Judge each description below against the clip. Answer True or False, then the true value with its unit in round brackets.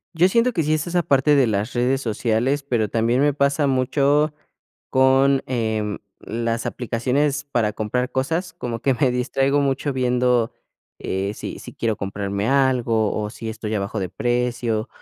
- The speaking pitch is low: True (125 Hz)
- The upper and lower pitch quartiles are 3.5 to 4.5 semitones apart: True (3.8 semitones)